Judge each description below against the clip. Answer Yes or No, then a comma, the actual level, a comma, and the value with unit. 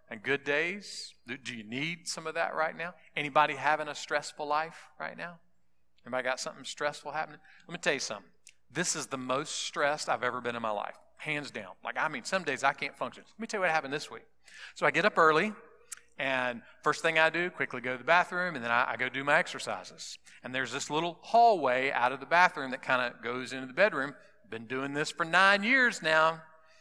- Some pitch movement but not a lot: Yes, average, 4.2 semitones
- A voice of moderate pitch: Yes, medium, 150 Hz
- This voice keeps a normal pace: No, fast, 230 wpm